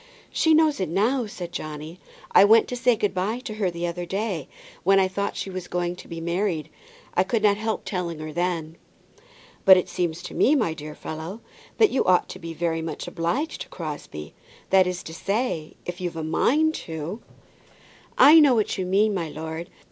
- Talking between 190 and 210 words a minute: Yes, fast, 205 wpm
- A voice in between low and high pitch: Yes, medium, 180 Hz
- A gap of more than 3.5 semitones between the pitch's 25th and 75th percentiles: Yes, average, 4.5 semitones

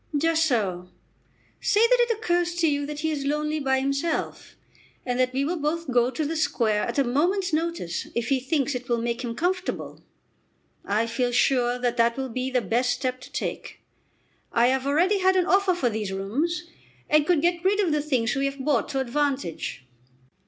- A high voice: Yes, very high, 275 Hz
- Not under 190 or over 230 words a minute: Yes, average, 200 wpm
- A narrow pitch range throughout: No, average, 5.2 semitones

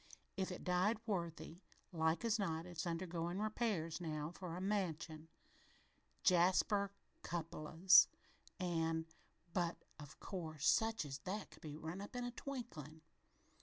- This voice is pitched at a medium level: Yes, medium, 175 Hz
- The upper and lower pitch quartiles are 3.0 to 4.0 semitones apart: Yes, average, 3.6 semitones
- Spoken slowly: Yes, slow, 130 wpm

